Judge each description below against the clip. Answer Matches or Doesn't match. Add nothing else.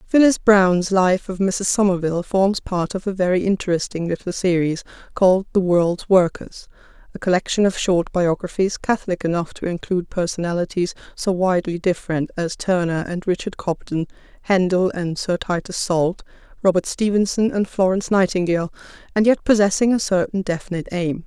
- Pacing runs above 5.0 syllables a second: Matches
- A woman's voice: Matches